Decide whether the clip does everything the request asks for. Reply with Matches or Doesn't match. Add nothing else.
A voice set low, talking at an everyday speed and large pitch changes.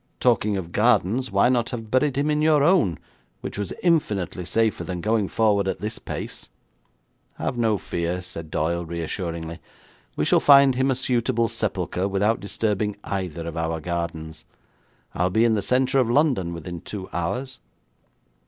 Matches